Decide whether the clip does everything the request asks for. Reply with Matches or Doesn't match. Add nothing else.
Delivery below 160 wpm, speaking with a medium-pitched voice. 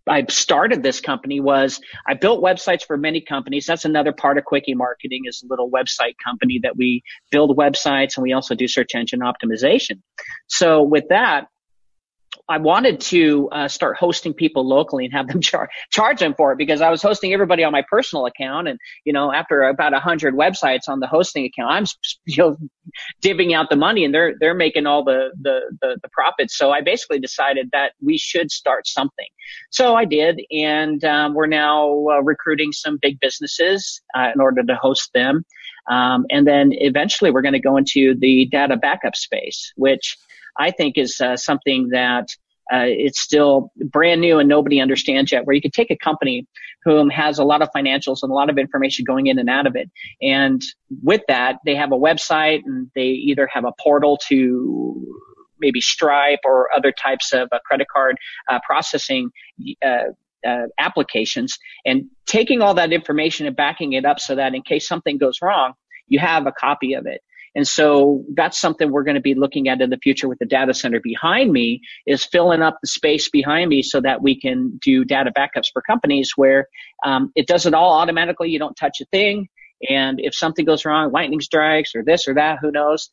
Doesn't match